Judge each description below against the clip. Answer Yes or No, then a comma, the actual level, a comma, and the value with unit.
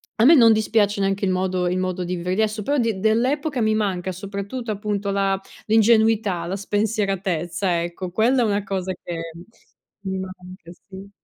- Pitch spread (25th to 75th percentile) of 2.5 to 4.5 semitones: Yes, average, 2.8 semitones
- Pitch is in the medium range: No, high, 200 Hz